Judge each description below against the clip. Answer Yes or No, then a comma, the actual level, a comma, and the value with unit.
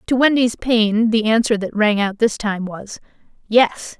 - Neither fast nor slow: Yes, average, 180 wpm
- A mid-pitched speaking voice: No, high, 220 Hz